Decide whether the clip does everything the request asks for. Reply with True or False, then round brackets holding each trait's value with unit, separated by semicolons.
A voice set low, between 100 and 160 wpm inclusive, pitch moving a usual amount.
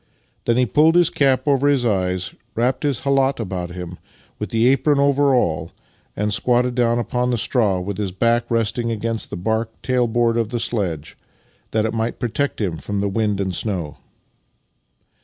False (115 Hz; 180 wpm; 3.9 semitones)